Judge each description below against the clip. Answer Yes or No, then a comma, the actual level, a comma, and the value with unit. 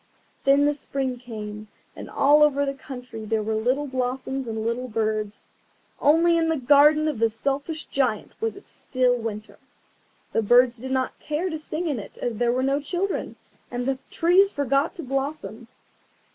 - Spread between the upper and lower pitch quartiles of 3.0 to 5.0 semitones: Yes, average, 3.9 semitones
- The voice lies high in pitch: Yes, very high, 265 Hz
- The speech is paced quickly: No, average, 175 wpm